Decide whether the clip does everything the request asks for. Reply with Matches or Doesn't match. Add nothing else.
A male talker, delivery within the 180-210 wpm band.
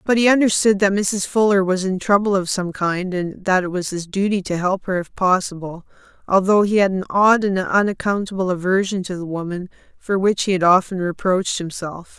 Doesn't match